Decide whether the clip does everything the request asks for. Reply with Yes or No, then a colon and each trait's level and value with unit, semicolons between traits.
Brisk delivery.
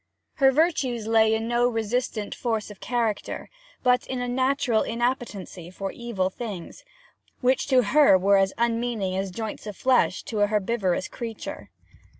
No: average, 155 wpm